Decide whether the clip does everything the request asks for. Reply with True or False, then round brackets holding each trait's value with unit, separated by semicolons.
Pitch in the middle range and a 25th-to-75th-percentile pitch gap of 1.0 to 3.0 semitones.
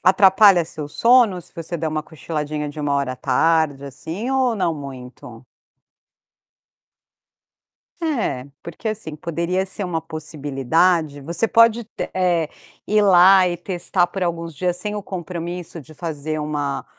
False (170 Hz; 3.7 semitones)